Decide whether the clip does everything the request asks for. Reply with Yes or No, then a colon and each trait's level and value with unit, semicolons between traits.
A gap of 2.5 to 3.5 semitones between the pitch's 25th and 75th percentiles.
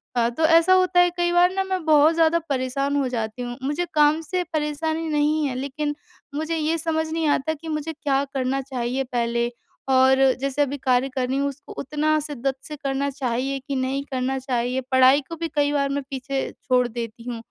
Yes: average, 3.2 semitones